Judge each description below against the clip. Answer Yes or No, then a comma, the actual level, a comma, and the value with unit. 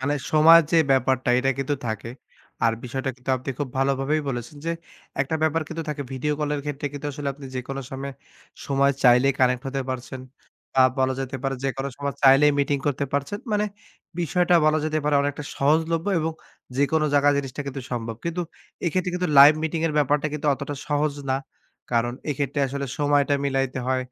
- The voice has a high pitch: No, medium, 140 Hz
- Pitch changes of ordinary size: No, narrow, 2.1 semitones